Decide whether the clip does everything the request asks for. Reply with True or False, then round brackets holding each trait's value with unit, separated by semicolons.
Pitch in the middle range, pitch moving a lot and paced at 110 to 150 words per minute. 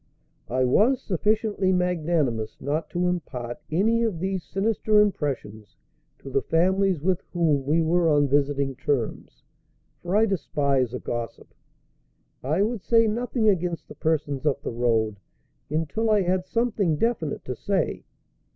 True (165 Hz; 6.1 semitones; 140 wpm)